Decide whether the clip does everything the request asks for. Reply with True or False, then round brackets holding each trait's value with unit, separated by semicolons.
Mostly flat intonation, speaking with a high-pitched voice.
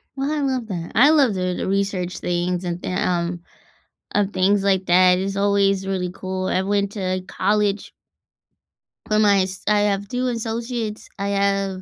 True (2.1 semitones; 195 Hz)